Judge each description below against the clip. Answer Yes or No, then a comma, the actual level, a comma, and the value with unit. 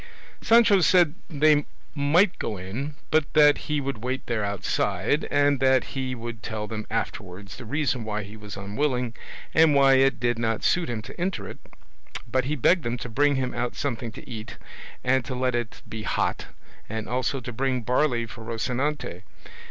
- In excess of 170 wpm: Yes, average, 185 wpm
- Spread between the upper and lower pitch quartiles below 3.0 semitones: No, average, 4.3 semitones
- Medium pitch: No, low, 125 Hz